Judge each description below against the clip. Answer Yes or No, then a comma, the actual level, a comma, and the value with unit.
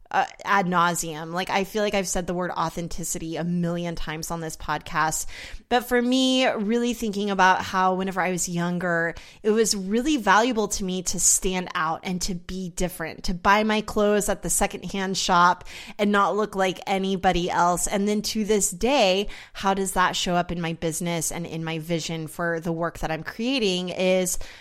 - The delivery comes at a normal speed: Yes, average, 195 wpm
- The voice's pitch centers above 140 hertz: Yes, medium, 185 Hz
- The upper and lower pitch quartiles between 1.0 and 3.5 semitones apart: Yes, average, 3.2 semitones